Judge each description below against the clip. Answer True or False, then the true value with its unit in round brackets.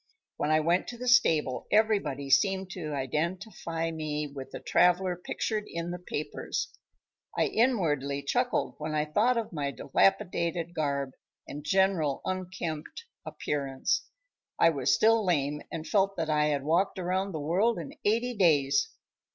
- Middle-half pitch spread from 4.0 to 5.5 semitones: True (4.6 semitones)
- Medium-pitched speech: True (165 Hz)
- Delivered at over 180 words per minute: False (150 wpm)